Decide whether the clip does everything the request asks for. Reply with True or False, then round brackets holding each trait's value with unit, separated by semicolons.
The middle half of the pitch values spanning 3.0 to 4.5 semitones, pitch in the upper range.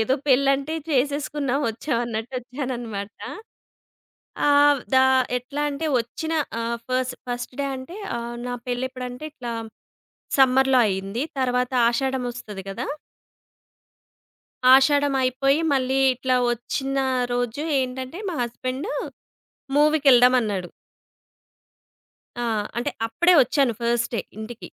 False (2.5 semitones; 255 Hz)